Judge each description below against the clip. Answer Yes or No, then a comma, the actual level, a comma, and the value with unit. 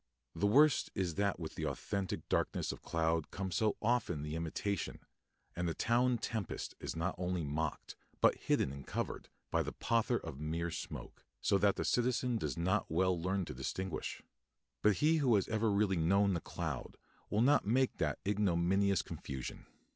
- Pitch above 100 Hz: No, very low, 95 Hz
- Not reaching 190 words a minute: Yes, average, 175 wpm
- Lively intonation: No, average, 4.6 semitones